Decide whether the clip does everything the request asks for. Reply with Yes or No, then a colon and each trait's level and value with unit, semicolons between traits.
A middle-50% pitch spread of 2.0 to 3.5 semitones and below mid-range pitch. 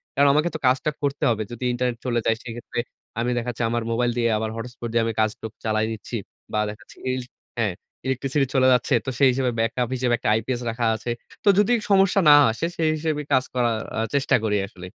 Yes: average, 2.8 semitones; low, 120 Hz